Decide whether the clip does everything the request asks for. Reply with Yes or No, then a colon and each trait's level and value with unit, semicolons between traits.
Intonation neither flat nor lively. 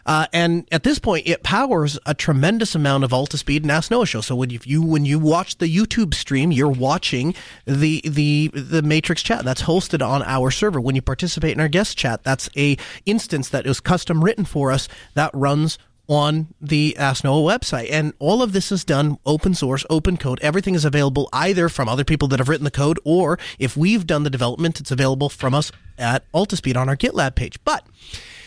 Yes: average, 3.8 semitones